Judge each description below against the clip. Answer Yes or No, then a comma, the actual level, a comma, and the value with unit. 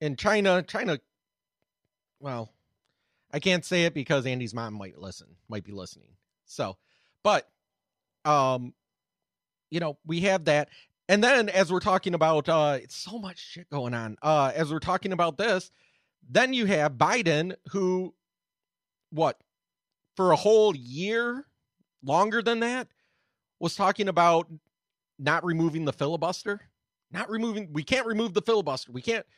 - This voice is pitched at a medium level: Yes, medium, 170 Hz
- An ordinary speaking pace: Yes, average, 145 wpm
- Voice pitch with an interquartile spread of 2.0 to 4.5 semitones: No, average, 5.2 semitones